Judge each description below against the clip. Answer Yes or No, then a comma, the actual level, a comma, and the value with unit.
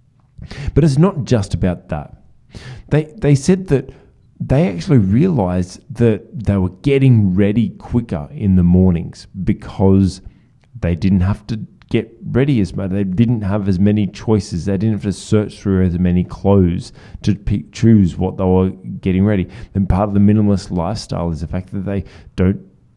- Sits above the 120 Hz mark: No, low, 100 Hz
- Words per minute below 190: Yes, average, 175 wpm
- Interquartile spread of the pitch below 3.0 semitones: No, average, 3.6 semitones